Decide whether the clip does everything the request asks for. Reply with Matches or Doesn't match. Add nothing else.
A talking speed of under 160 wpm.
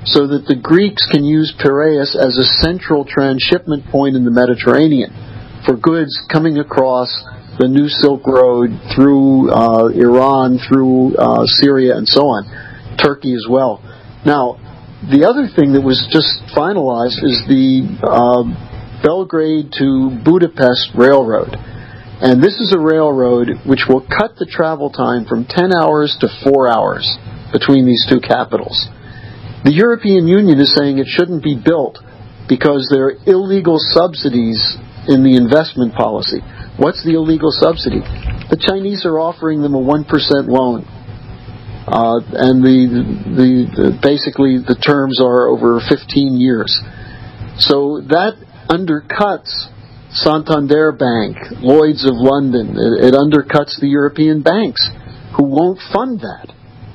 Matches